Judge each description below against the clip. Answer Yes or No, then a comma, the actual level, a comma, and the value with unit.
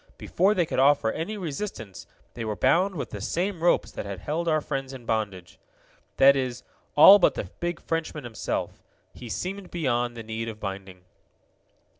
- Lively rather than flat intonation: Yes, wide, 7.3 semitones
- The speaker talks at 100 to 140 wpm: No, average, 175 wpm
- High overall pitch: No, low, 135 Hz